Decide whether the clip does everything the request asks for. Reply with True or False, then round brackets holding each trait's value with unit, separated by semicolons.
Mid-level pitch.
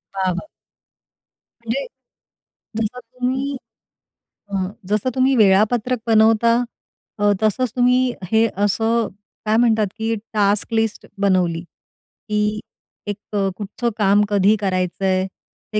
False (215 Hz)